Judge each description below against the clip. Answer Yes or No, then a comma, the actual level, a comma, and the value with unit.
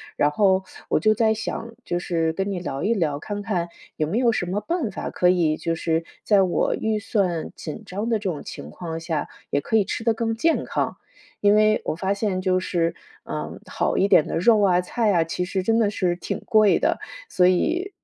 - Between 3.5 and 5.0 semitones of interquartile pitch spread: Yes, average, 4.0 semitones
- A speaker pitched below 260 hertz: Yes, high, 190 Hz